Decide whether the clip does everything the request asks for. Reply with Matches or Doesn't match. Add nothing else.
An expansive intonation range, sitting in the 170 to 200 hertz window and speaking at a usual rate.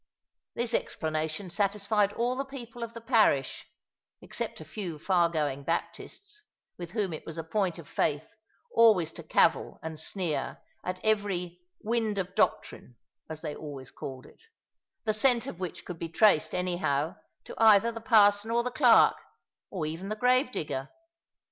Matches